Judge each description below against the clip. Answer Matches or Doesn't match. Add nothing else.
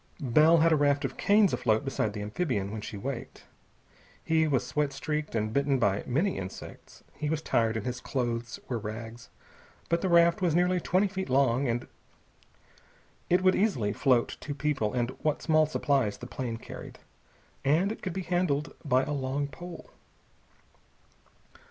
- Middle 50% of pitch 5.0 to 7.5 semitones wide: Matches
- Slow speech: Doesn't match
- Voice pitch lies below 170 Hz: Matches